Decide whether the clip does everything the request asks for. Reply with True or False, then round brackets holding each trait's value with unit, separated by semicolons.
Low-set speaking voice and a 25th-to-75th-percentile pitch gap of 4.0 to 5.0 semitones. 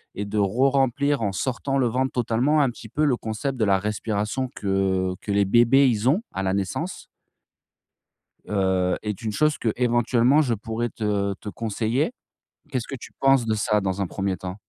True (110 Hz; 4.7 semitones)